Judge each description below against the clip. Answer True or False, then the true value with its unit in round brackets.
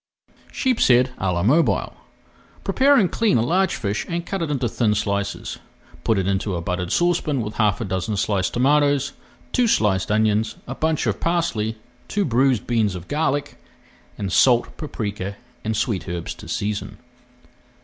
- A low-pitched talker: True (115 Hz)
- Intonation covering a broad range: True (6.7 semitones)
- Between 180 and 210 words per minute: False (165 wpm)